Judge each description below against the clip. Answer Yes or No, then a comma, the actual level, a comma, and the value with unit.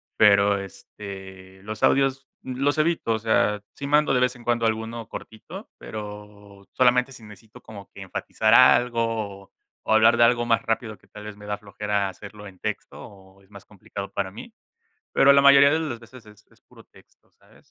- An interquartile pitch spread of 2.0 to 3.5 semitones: Yes, average, 3.2 semitones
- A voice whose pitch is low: Yes, low, 110 Hz